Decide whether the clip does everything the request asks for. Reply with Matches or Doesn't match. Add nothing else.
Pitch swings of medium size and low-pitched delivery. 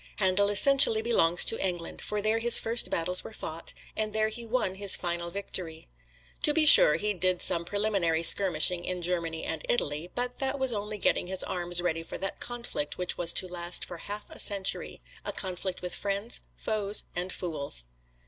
Doesn't match